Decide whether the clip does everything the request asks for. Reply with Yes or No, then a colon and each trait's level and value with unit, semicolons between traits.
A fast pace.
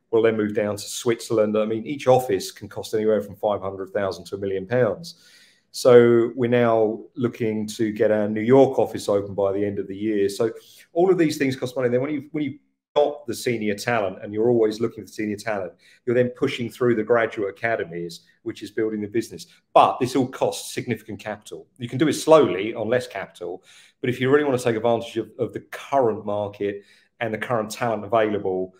Yes: fast, 215 wpm